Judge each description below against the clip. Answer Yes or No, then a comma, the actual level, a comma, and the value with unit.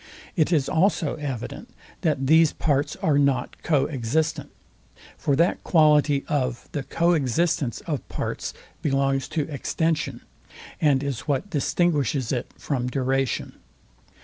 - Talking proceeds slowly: Yes, slow, 125 wpm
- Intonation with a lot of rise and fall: No, average, 3.0 semitones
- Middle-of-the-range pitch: Yes, medium, 145 Hz